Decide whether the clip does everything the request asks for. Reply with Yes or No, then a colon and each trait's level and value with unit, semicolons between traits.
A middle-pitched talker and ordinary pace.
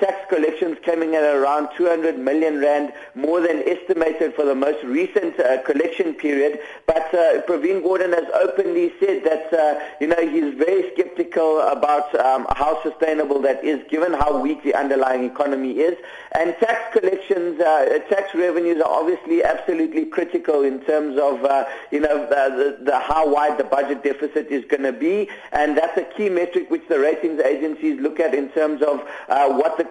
Yes: medium, 155 Hz; average, 180 wpm